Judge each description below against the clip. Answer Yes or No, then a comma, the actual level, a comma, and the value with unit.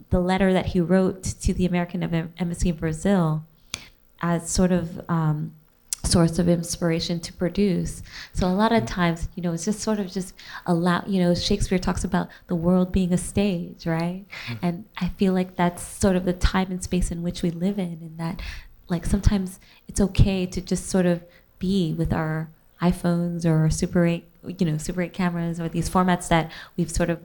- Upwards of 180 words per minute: Yes, average, 200 wpm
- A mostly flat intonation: Yes, narrow, 1.5 semitones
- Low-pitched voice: No, medium, 175 Hz